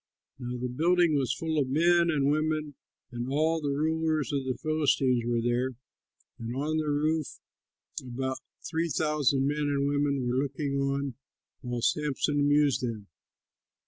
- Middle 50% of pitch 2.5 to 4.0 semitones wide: Yes, average, 3.0 semitones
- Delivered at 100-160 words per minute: Yes, average, 150 wpm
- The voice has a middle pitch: Yes, medium, 145 Hz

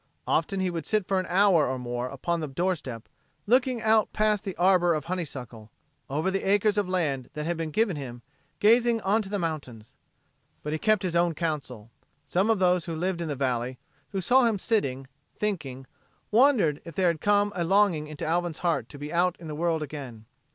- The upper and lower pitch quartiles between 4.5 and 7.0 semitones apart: Yes, average, 5.3 semitones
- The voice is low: No, medium, 170 Hz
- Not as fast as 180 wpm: No, fast, 205 wpm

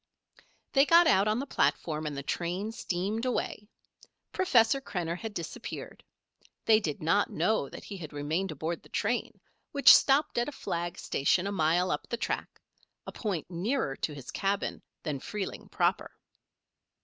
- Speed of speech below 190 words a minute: Yes, average, 160 wpm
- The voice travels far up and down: Yes, wide, 5.7 semitones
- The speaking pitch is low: No, high, 190 Hz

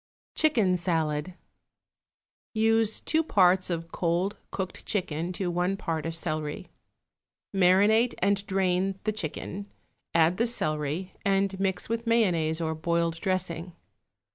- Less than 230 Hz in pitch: Yes, medium, 185 Hz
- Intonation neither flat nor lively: Yes, average, 3.2 semitones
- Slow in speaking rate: Yes, slow, 120 wpm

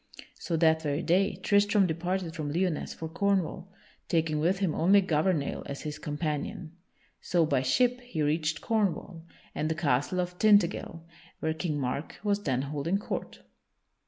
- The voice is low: No, medium, 165 Hz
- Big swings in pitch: No, average, 3.8 semitones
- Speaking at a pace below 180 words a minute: Yes, average, 155 wpm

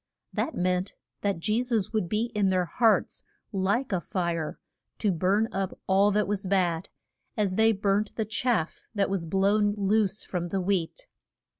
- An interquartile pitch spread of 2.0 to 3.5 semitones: Yes, narrow, 2.5 semitones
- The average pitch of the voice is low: No, high, 195 Hz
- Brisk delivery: No, average, 165 wpm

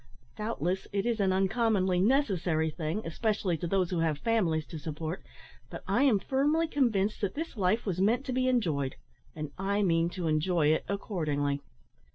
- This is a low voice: No, high, 190 Hz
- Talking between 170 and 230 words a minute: Yes, average, 175 wpm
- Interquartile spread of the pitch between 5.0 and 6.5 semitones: Yes, wide, 5.4 semitones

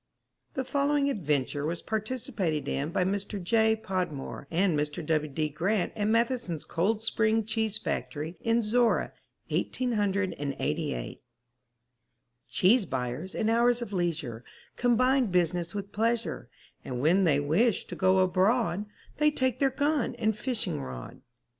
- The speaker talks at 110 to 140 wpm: Yes, slow, 135 wpm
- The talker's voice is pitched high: Yes, high, 200 Hz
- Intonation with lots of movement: Yes, wide, 6.3 semitones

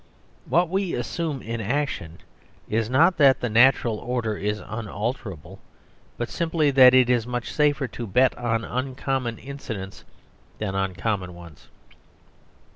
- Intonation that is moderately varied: Yes, average, 4.2 semitones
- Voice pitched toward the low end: Yes, low, 120 Hz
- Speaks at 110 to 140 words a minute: Yes, slow, 135 wpm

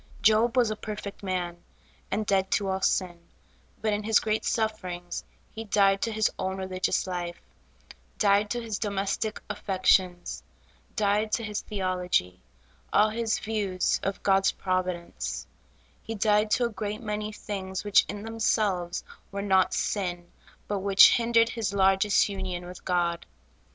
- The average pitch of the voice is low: No, high, 200 Hz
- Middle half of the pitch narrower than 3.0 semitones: Yes, narrow, 2.6 semitones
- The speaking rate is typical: Yes, average, 145 wpm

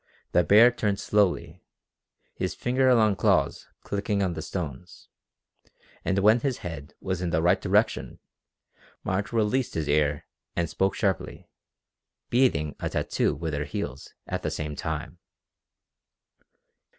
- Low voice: Yes, very low, 90 Hz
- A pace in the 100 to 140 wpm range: Yes, slow, 135 wpm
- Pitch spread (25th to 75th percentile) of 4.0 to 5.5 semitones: Yes, average, 4.9 semitones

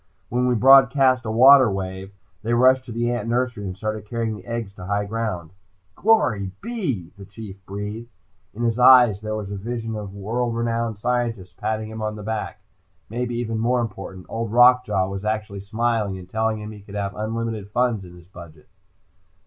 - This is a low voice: Yes, low, 110 Hz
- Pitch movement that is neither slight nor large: Yes, average, 3.0 semitones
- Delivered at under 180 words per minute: No, average, 190 wpm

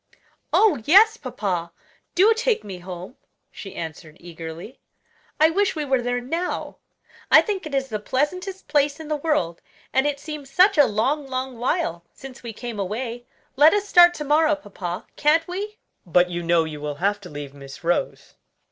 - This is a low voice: No, very high, 260 Hz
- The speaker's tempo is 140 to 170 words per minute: No, average, 180 wpm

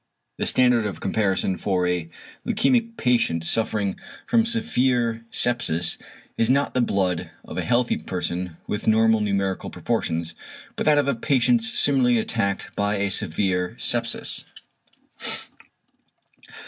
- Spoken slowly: Yes, slow, 125 wpm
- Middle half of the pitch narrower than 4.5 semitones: No, average, 5.1 semitones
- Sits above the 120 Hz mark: No, low, 110 Hz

